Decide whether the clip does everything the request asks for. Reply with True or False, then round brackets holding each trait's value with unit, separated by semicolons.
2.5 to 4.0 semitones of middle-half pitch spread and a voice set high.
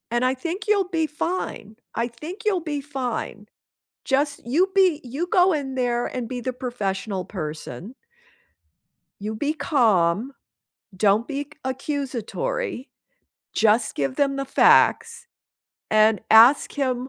False (5.5 semitones; 260 Hz)